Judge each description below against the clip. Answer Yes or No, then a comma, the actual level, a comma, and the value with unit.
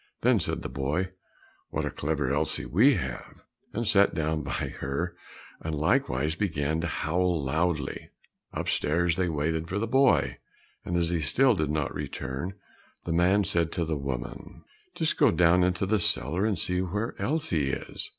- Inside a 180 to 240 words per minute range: No, average, 170 wpm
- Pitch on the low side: Yes, very low, 85 Hz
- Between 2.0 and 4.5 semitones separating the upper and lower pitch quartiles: Yes, average, 3.7 semitones